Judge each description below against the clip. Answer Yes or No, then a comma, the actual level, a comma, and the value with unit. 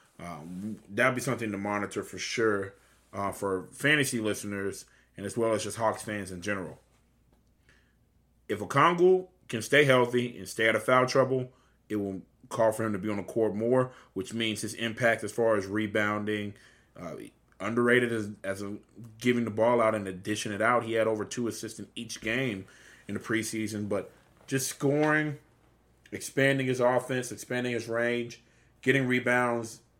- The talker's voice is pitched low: Yes, low, 110 Hz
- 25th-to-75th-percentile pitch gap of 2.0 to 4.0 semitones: Yes, average, 3.1 semitones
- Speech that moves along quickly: No, average, 175 wpm